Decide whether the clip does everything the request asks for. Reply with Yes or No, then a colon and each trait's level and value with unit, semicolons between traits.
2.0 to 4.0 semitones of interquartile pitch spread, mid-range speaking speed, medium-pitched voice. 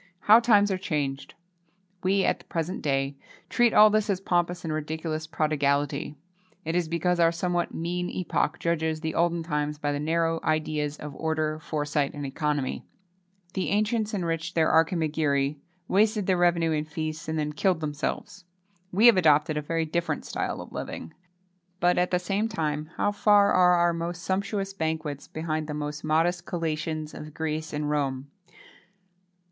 Yes: average, 2.8 semitones; average, 165 wpm; medium, 160 Hz